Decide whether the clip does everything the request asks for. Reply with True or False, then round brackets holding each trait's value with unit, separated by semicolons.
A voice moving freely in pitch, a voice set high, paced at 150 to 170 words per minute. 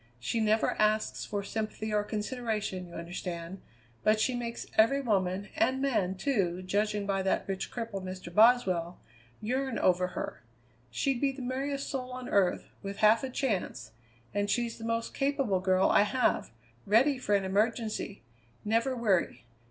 False (4.4 semitones; 215 Hz; 160 wpm)